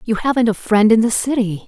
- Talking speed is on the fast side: Yes, fast, 250 wpm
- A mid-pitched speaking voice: No, high, 225 Hz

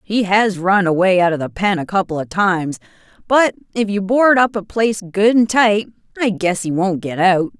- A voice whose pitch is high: Yes, high, 195 Hz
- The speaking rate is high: Yes, fast, 220 wpm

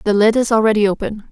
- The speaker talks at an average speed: No, fast, 230 wpm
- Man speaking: No, female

